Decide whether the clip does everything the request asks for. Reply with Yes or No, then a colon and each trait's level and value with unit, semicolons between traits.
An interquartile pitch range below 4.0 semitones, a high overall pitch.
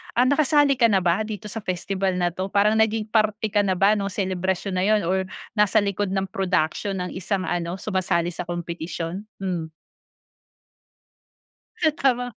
Yes: average, 2.9 semitones; high, 195 Hz